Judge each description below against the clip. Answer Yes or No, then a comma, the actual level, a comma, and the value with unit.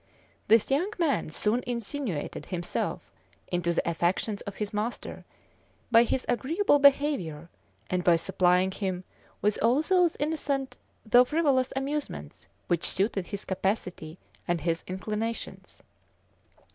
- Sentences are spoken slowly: Yes, slow, 120 wpm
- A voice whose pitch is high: Yes, high, 210 Hz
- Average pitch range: No, wide, 7.1 semitones